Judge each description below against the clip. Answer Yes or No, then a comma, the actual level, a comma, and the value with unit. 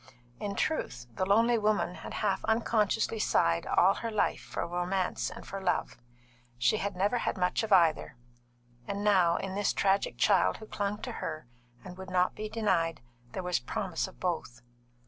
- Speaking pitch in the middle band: No, high, 195 Hz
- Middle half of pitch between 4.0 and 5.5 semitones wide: No, average, 2.9 semitones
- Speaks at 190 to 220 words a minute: No, average, 175 wpm